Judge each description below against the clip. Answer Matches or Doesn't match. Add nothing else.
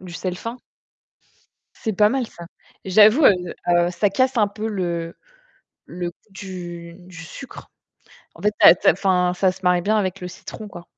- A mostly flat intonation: Doesn't match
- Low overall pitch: Doesn't match